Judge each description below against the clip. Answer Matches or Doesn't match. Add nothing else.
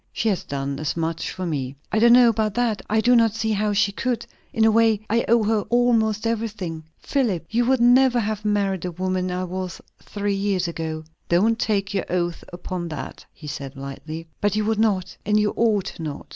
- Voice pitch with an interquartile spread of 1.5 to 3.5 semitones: Doesn't match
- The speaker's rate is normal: Doesn't match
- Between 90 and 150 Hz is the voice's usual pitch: Doesn't match